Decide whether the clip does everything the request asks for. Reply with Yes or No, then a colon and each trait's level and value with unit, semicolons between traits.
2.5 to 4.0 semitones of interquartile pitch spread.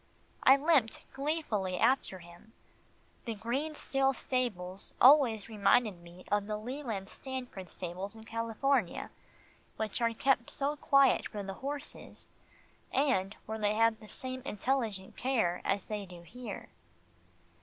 No: average, 5.1 semitones